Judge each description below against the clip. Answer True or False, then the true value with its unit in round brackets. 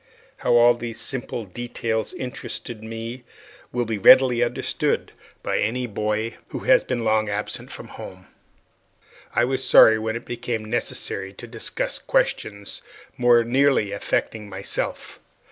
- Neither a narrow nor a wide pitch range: False (2.0 semitones)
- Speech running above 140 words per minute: False (135 wpm)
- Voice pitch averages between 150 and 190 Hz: False (115 Hz)